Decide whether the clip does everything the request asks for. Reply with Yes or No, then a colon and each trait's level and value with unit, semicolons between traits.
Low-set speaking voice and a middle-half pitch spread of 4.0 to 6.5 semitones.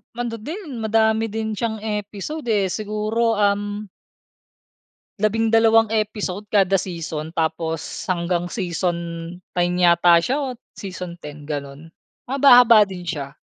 No: high, 205 Hz; average, 4.5 semitones